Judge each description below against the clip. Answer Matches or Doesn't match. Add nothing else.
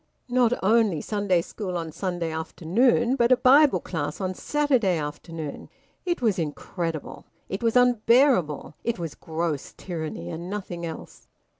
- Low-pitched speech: Doesn't match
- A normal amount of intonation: Doesn't match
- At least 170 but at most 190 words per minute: Doesn't match